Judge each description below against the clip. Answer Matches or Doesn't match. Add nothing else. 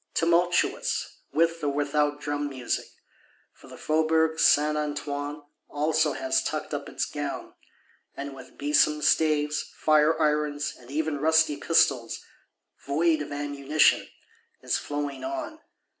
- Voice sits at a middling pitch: Matches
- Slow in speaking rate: Matches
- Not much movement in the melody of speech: Matches